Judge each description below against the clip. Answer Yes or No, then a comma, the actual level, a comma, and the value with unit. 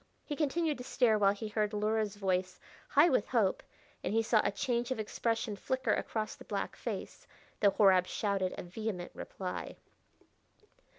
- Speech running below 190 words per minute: Yes, average, 165 wpm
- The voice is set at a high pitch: Yes, high, 215 Hz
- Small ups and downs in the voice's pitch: No, average, 3.4 semitones